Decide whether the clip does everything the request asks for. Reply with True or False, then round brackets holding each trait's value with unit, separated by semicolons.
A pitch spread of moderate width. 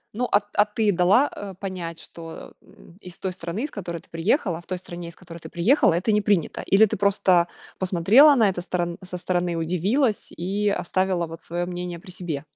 True (3.0 semitones)